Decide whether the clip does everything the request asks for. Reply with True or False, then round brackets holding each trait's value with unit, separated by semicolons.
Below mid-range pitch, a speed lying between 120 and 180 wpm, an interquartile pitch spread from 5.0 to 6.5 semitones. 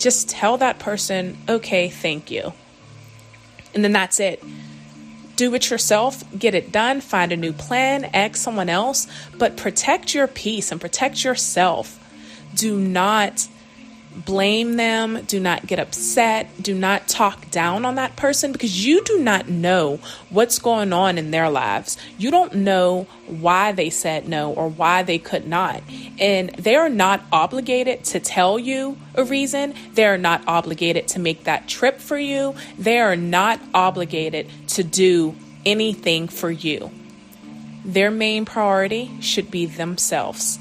False (195 Hz; 155 wpm; 5.6 semitones)